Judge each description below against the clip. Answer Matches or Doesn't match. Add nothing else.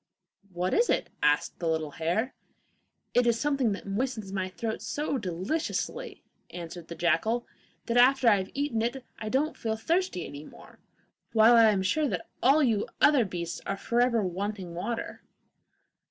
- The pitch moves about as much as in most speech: Doesn't match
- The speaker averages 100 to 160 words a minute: Doesn't match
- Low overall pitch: Doesn't match